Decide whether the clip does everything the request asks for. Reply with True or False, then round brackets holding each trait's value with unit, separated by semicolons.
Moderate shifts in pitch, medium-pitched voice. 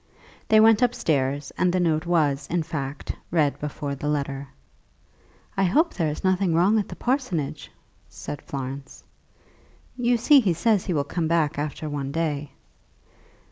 True (4.8 semitones; 160 Hz)